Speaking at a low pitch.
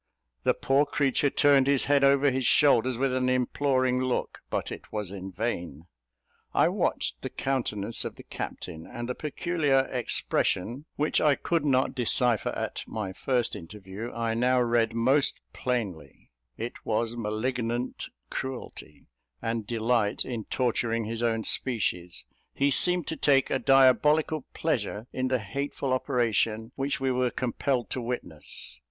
Yes: low, 125 Hz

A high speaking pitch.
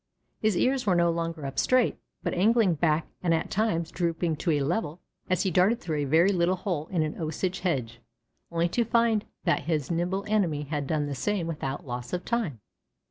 No: medium, 170 Hz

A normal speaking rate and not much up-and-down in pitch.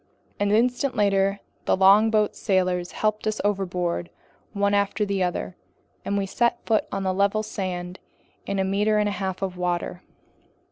Yes: average, 155 wpm; narrow, 2.1 semitones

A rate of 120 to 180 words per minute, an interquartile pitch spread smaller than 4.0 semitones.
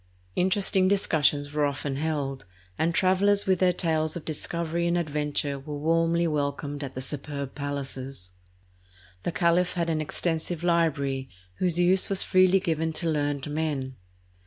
Yes: average, 145 wpm; average, 3.3 semitones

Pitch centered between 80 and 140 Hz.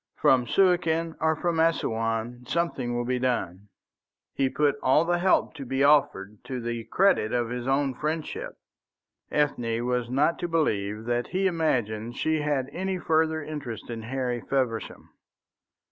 Yes: low, 135 Hz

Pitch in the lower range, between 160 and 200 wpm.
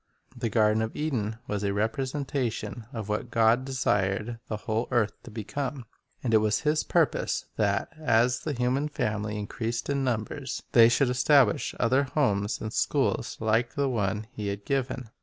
Yes: low, 115 Hz; average, 170 wpm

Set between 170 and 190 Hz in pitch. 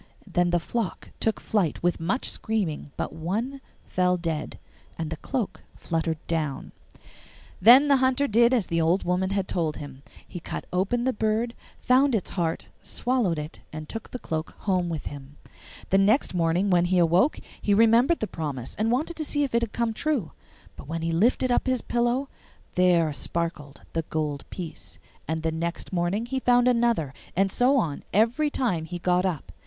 Yes: medium, 185 Hz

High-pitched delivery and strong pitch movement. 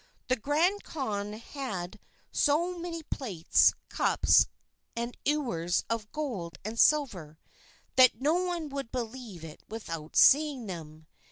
Yes: high, 240 Hz; wide, 7.9 semitones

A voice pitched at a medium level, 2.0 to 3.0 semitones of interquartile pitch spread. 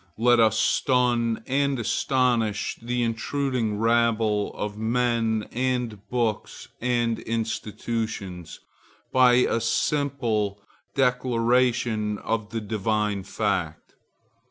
No: low, 115 Hz; narrow, 2.4 semitones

